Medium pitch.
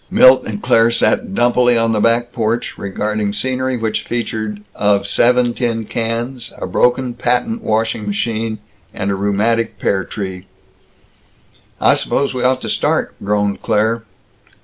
No: low, 115 Hz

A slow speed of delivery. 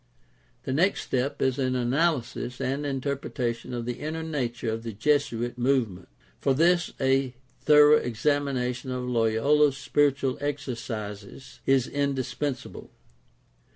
Yes: slow, 120 wpm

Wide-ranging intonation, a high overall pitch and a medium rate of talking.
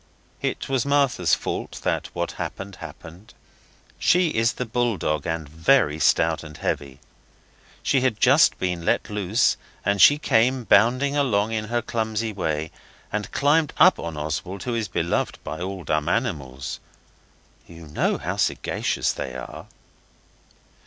No: wide, 7.1 semitones; low, 100 Hz; average, 145 wpm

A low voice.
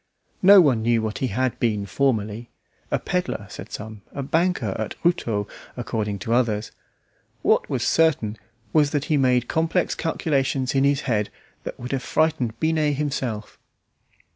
Yes: low, 130 Hz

